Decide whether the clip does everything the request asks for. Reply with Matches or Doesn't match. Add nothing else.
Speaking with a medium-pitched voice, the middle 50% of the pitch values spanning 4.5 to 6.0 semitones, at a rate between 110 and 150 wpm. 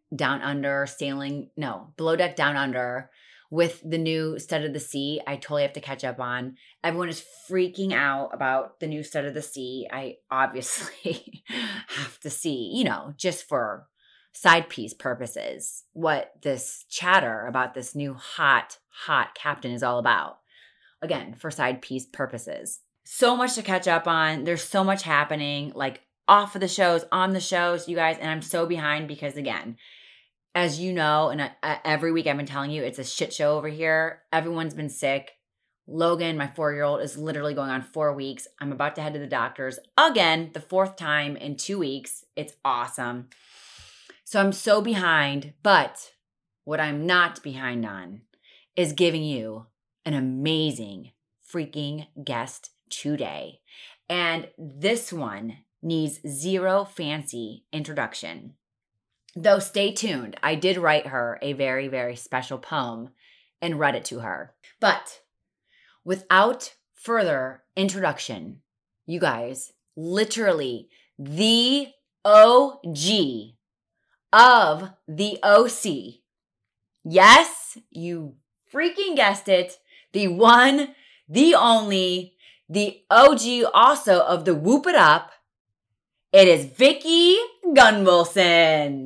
Matches